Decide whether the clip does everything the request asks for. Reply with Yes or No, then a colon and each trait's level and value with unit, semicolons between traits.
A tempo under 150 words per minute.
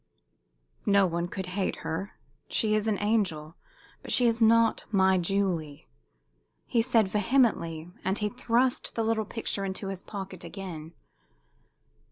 Yes: average, 140 wpm